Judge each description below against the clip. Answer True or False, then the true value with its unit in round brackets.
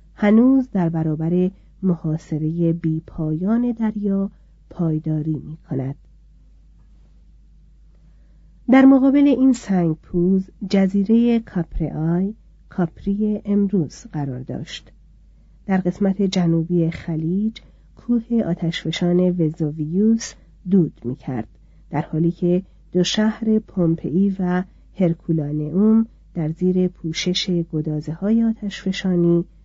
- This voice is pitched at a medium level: True (180 Hz)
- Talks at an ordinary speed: False (90 wpm)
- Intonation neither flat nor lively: True (3.9 semitones)